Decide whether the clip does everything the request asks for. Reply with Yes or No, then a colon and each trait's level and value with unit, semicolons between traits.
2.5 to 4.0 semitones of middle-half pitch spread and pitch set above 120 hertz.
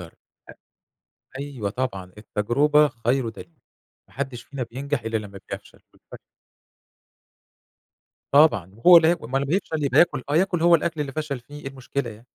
No: average, 4.6 semitones; low, 135 Hz